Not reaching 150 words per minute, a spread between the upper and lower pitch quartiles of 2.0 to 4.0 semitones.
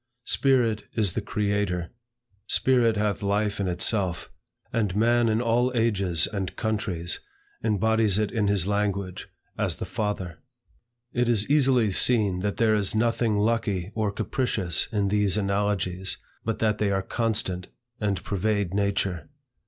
Yes: average, 140 wpm; narrow, 2.5 semitones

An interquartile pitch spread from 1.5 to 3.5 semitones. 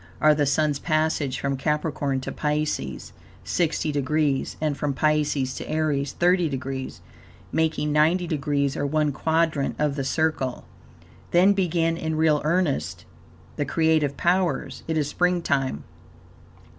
Yes: narrow, 2.4 semitones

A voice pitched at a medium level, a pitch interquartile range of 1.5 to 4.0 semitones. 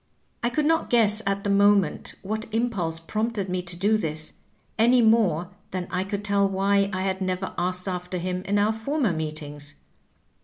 No: high, 195 Hz; average, 3.2 semitones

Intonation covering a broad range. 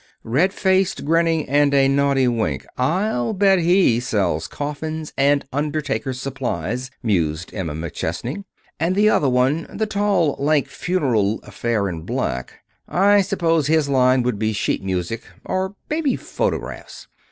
Yes: wide, 6.8 semitones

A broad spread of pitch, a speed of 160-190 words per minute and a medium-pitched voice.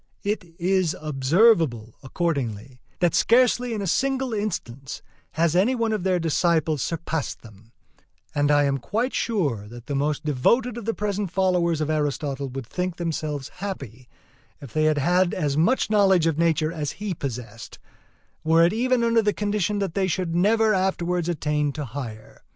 Yes: wide, 5.9 semitones; average, 165 wpm; medium, 165 Hz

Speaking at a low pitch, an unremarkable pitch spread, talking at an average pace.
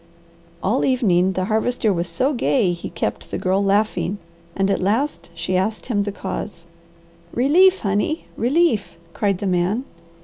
No: high, 205 Hz; average, 5.0 semitones; average, 150 wpm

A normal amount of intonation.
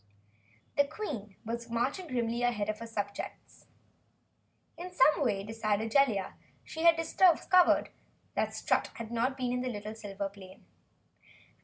Yes: average, 4.9 semitones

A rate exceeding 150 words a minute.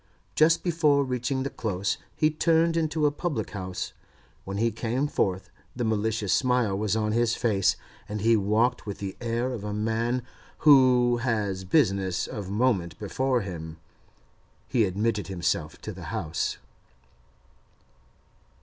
No: average, 140 wpm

